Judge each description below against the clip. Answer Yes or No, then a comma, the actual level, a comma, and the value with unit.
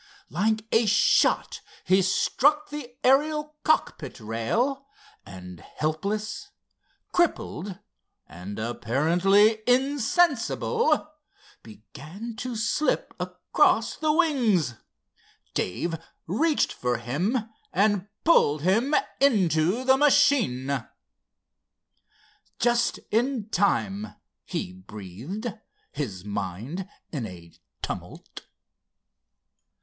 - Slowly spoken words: Yes, slow, 80 wpm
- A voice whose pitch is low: No, high, 200 Hz